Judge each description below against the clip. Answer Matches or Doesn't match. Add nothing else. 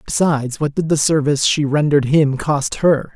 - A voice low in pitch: Doesn't match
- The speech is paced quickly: Doesn't match